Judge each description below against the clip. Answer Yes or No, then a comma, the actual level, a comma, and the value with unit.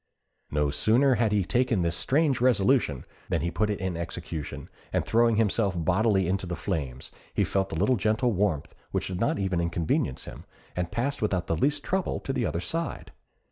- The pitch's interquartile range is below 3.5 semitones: No, wide, 5.6 semitones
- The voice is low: Yes, low, 100 Hz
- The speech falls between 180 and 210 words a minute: Yes, average, 190 wpm